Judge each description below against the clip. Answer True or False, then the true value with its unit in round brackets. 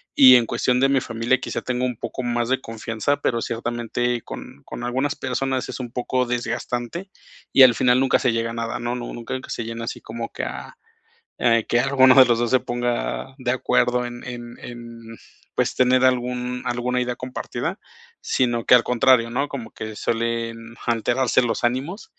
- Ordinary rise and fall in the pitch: False (1.5 semitones)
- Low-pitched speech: True (120 Hz)